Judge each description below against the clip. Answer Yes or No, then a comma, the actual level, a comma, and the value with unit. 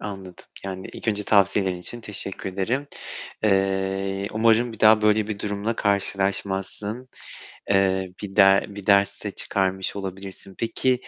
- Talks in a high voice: No, low, 100 Hz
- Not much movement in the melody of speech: Yes, narrow, 1.8 semitones